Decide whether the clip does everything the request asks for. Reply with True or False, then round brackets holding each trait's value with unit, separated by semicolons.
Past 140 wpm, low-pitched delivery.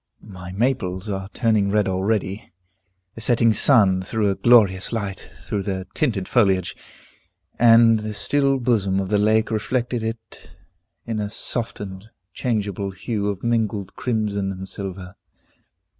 False (135 wpm; 105 Hz)